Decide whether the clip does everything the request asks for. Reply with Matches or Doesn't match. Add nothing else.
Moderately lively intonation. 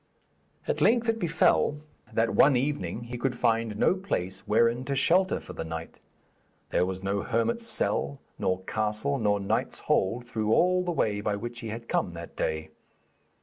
Doesn't match